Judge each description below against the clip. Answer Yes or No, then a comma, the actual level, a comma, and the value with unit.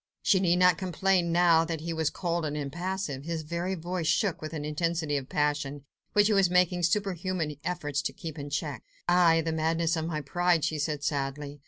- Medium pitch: Yes, medium, 165 Hz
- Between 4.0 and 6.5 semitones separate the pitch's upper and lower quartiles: No, average, 3.0 semitones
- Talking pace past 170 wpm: Yes, average, 200 wpm